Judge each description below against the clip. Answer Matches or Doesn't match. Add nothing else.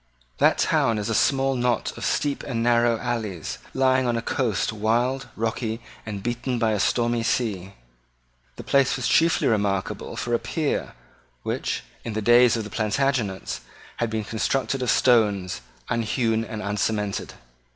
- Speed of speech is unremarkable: Matches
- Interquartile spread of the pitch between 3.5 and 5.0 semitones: Doesn't match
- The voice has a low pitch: Matches